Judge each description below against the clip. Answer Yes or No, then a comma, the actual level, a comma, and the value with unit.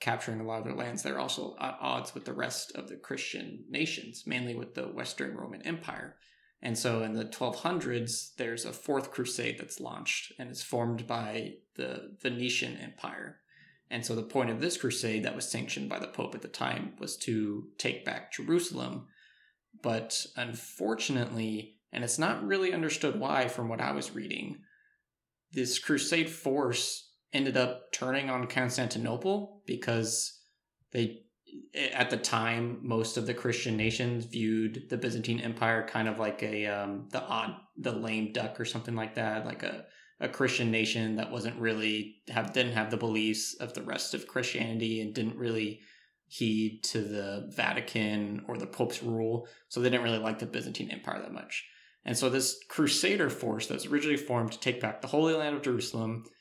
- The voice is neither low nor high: No, low, 115 Hz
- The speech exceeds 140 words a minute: Yes, average, 180 wpm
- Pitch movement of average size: No, narrow, 2.2 semitones